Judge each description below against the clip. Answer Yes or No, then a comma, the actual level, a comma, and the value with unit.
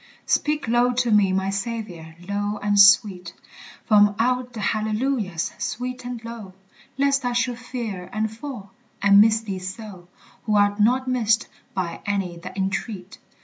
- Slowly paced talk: No, average, 150 wpm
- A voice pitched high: Yes, high, 215 Hz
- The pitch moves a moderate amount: Yes, average, 3.7 semitones